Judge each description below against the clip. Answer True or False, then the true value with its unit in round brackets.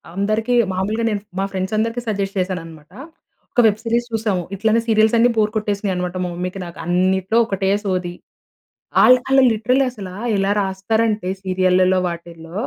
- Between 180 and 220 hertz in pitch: True (195 Hz)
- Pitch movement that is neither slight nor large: True (3.1 semitones)